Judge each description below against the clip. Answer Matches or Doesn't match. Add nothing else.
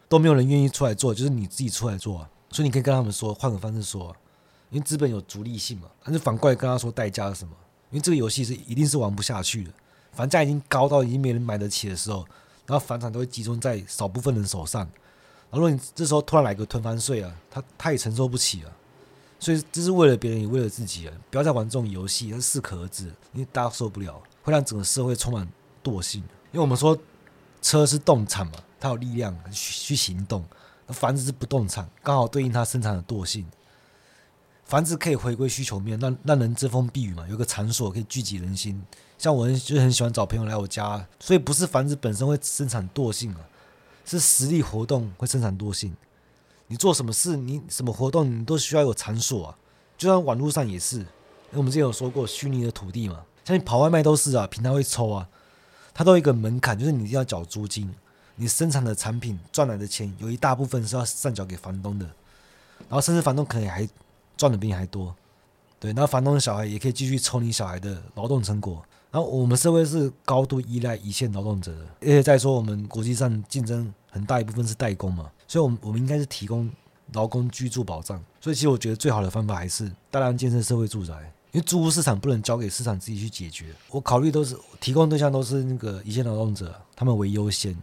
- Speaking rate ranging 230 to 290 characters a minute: Doesn't match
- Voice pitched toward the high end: Doesn't match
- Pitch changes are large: Doesn't match